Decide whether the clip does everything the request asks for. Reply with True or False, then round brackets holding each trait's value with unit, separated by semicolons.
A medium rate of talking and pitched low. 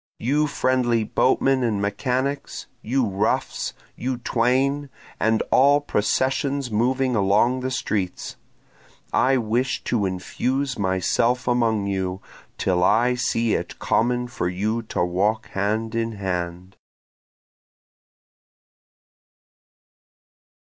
False (100 wpm; 115 Hz)